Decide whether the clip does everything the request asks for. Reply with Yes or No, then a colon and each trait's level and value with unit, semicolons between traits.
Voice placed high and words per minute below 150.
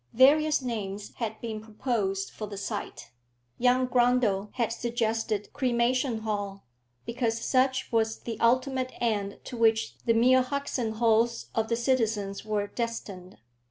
Yes: high, 230 Hz; average, 140 wpm